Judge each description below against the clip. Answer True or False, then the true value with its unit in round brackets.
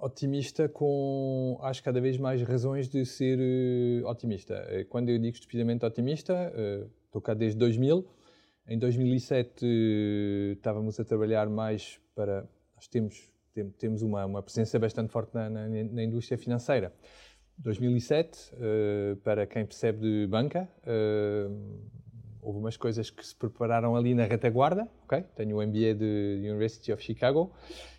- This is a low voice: True (115 Hz)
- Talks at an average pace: True (150 wpm)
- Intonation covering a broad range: False (2.8 semitones)